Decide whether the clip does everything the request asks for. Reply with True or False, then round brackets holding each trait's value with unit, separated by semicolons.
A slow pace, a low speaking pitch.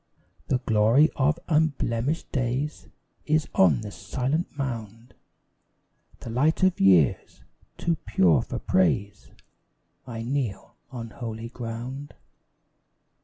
True (105 wpm; 120 Hz)